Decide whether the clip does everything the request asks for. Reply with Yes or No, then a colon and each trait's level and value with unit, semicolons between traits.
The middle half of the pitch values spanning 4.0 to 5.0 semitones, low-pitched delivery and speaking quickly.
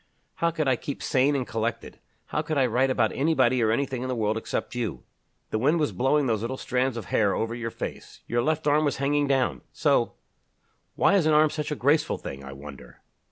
Yes: average, 4.3 semitones; low, 130 Hz; fast, 220 wpm